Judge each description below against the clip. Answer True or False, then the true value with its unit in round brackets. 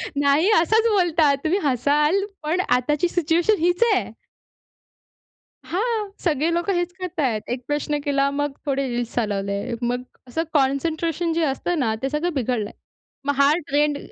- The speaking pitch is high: True (295 Hz)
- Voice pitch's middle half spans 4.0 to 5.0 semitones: True (4.4 semitones)